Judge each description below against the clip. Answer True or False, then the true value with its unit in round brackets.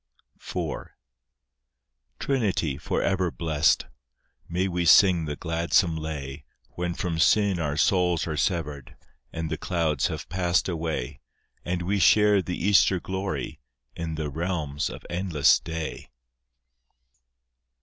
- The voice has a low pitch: True (85 Hz)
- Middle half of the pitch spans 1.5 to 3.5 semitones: True (2.7 semitones)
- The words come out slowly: True (120 wpm)